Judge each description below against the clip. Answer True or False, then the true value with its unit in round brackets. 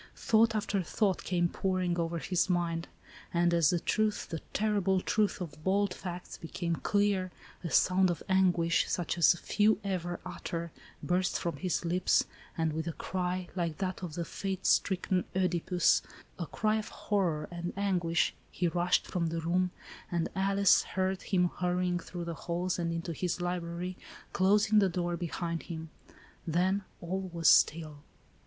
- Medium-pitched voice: True (180 Hz)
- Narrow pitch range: True (2.0 semitones)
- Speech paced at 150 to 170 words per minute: True (165 wpm)